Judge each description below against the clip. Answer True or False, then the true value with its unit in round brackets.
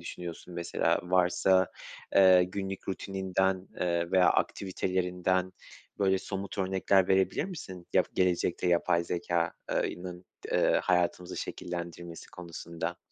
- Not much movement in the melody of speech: True (1.5 semitones)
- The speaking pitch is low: True (90 Hz)